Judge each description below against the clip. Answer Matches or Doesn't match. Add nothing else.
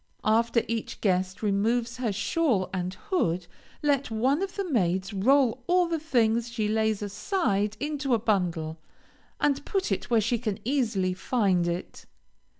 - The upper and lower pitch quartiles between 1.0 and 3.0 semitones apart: Doesn't match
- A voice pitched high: Matches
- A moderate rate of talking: Matches